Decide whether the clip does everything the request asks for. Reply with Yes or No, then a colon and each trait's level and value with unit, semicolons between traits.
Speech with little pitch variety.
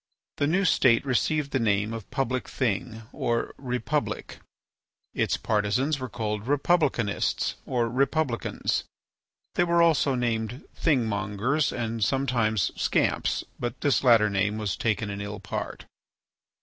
No: average, 4.3 semitones